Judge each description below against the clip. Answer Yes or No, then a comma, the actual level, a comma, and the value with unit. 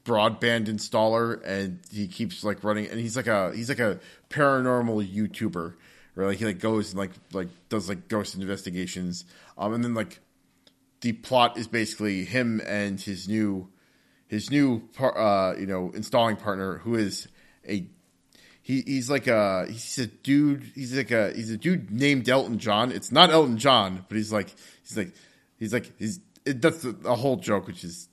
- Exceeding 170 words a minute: Yes, average, 185 wpm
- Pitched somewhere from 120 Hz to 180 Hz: No, low, 110 Hz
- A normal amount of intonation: Yes, average, 3.6 semitones